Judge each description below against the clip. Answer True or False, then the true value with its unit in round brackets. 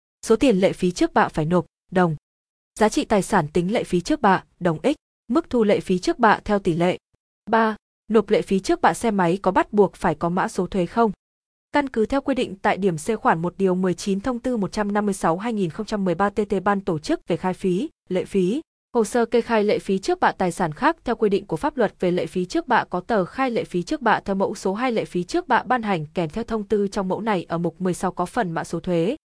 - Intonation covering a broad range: False (4.1 semitones)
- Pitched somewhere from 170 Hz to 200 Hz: True (195 Hz)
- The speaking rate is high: True (255 wpm)